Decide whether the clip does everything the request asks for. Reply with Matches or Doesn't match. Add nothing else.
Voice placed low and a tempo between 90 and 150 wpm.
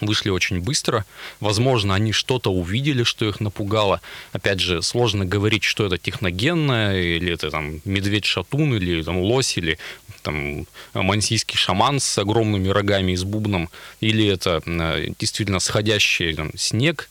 Matches